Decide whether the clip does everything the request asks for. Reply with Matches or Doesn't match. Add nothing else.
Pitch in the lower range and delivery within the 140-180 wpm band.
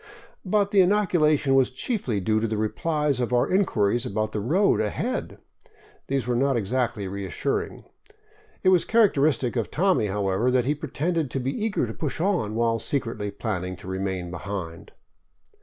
Matches